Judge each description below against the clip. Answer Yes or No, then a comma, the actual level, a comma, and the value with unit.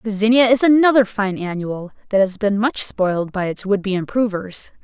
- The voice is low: No, high, 210 Hz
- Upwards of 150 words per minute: Yes, average, 200 wpm